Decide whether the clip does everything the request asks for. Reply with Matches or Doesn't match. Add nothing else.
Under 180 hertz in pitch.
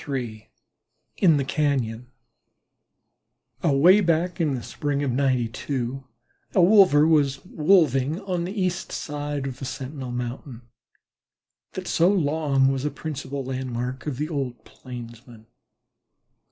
Matches